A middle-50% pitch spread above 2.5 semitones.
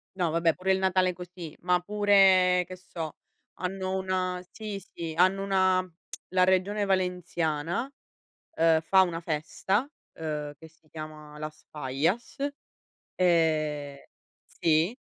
Yes: average, 2.9 semitones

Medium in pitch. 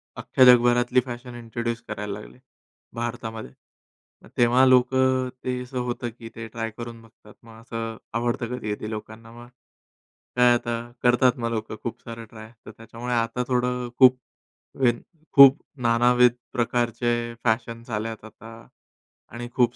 No: low, 120 Hz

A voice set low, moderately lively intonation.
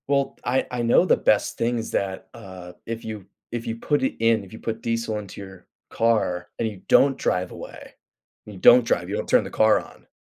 Yes: low, 115 Hz; average, 3.0 semitones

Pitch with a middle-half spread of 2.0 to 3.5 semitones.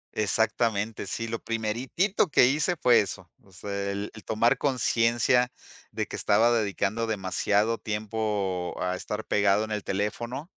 Yes: narrow, 2.6 semitones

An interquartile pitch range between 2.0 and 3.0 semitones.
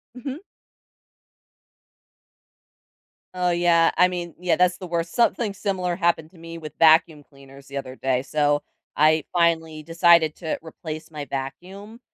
Yes: average, 2.7 semitones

